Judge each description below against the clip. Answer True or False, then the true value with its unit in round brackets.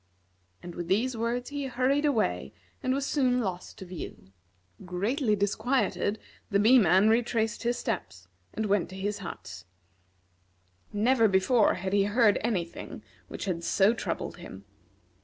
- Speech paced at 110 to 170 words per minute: True (150 wpm)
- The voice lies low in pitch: False (210 Hz)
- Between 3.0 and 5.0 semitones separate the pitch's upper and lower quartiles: True (4.5 semitones)